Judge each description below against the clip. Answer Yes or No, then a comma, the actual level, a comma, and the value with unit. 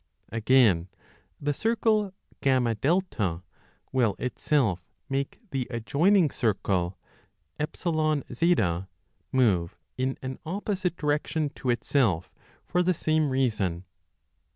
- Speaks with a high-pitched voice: No, low, 135 Hz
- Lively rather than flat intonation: Yes, wide, 6.2 semitones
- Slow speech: Yes, slow, 90 wpm